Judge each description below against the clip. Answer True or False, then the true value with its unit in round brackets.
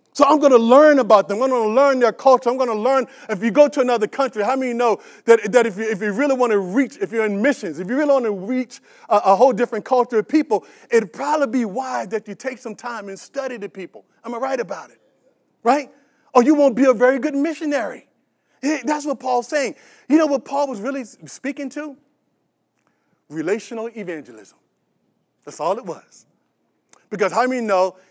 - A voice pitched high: True (255 Hz)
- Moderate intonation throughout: True (4.0 semitones)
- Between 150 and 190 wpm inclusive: False (205 wpm)